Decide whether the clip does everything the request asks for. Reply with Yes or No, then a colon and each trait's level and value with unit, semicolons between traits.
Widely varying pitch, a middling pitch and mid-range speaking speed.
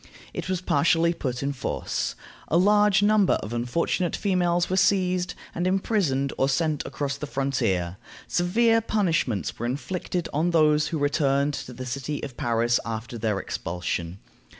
Yes: wide, 6.2 semitones; medium, 150 Hz; average, 150 wpm